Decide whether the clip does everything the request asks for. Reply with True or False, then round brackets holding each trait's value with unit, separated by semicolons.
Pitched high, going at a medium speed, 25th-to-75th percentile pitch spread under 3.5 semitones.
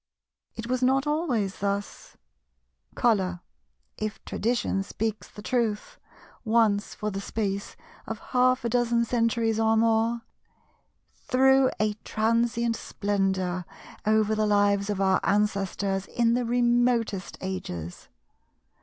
False (220 Hz; 115 wpm; 2.9 semitones)